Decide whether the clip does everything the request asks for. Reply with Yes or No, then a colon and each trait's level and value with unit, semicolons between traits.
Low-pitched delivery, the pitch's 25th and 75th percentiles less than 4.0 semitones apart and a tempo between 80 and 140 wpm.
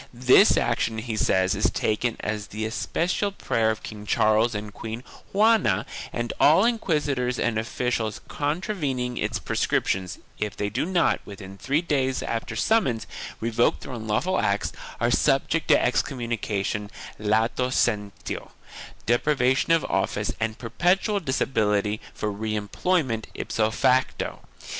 No: low, 115 Hz; average, 4.6 semitones; slow, 135 wpm